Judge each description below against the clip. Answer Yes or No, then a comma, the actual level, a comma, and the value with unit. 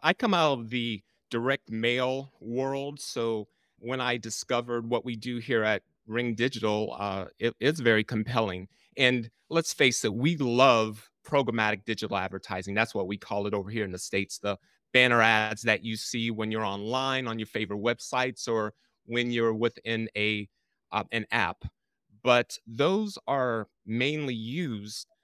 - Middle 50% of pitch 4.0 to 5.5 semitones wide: No, average, 2.7 semitones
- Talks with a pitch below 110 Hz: No, low, 115 Hz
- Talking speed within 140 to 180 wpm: Yes, average, 160 wpm